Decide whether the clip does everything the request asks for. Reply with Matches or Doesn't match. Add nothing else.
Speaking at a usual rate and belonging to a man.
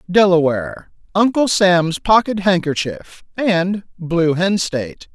Doesn't match